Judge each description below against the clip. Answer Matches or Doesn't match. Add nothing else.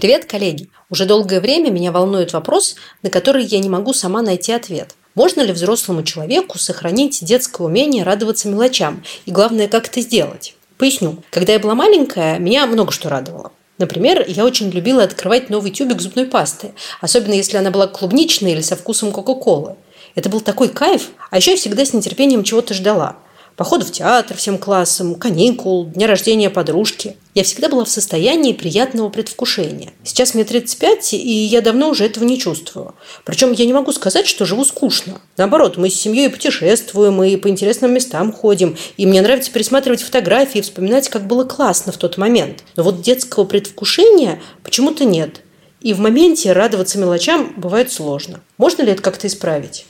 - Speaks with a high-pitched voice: Matches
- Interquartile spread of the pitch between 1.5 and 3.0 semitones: Doesn't match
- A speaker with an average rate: Doesn't match